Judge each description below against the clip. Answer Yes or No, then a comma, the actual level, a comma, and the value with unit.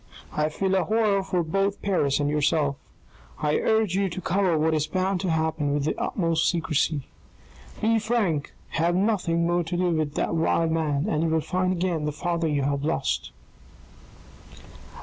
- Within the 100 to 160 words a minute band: No, average, 175 wpm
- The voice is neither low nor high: Yes, medium, 165 Hz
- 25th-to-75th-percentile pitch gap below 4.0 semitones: Yes, average, 3.6 semitones